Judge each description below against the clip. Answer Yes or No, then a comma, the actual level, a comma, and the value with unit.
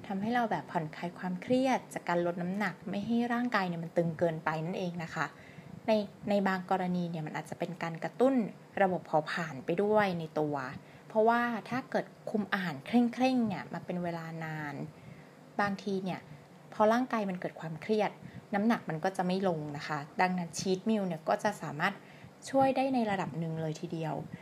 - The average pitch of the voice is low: No, medium, 180 Hz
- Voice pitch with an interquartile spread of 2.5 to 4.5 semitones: Yes, average, 4.1 semitones